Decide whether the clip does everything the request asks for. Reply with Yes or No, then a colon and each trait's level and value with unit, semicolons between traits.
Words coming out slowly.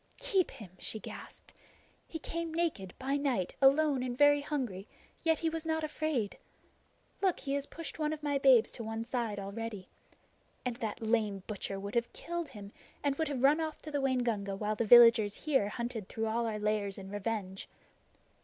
No: average, 185 wpm